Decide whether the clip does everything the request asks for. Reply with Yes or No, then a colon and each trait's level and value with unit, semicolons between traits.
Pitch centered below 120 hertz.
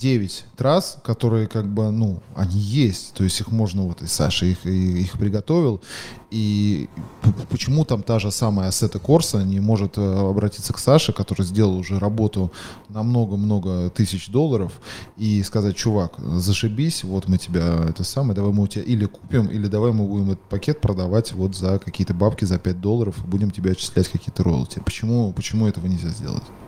Yes: low, 105 Hz